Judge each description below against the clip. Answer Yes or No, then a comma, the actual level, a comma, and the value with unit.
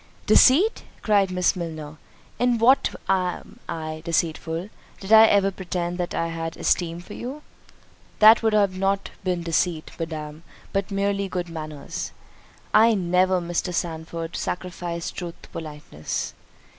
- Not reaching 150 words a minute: Yes, average, 140 wpm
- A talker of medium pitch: Yes, medium, 180 Hz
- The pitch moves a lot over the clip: No, average, 3.2 semitones